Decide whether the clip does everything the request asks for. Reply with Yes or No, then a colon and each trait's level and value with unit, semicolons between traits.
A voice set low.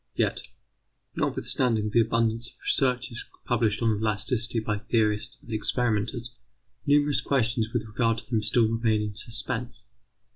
Yes: low, 115 Hz